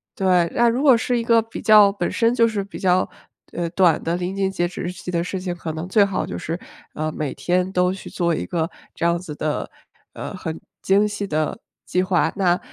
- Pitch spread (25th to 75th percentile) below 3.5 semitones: Yes, average, 2.8 semitones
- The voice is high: No, medium, 180 Hz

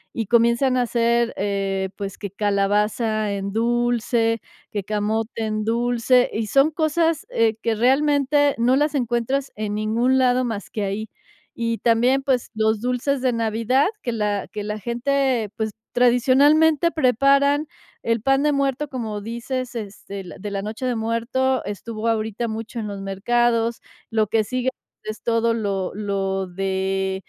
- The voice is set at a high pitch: Yes, high, 230 Hz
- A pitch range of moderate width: Yes, average, 3.3 semitones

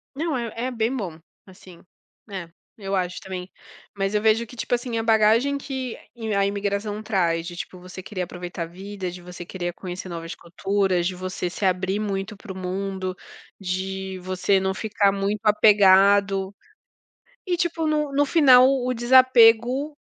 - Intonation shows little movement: No, average, 3.7 semitones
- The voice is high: Yes, high, 195 Hz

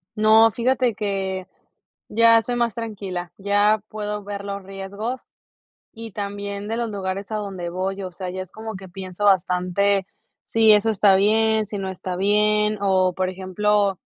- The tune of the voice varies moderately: No, narrow, 2.2 semitones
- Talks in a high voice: Yes, high, 200 Hz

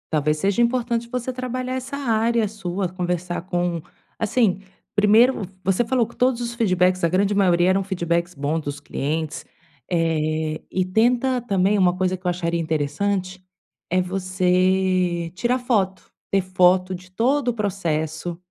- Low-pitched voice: No, medium, 185 Hz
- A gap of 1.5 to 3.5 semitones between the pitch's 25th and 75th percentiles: No, average, 4.6 semitones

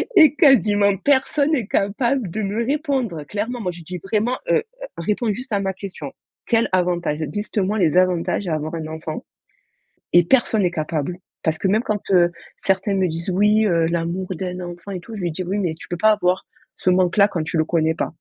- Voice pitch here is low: No, high, 190 Hz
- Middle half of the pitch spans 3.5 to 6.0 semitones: Yes, average, 3.9 semitones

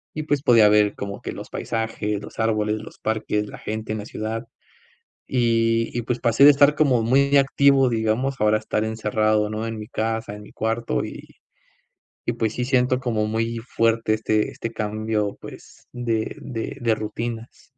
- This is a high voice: No, low, 115 Hz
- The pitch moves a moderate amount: No, narrow, 2.0 semitones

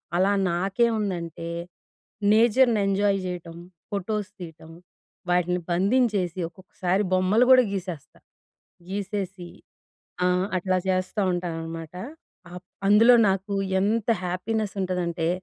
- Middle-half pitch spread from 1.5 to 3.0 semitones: Yes, average, 2.7 semitones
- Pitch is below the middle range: No, medium, 185 Hz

